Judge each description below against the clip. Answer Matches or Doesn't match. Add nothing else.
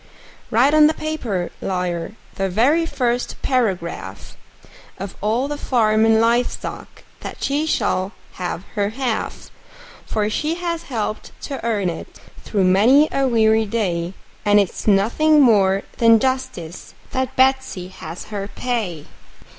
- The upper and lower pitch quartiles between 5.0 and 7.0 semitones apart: Matches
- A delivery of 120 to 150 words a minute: Matches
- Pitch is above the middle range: Matches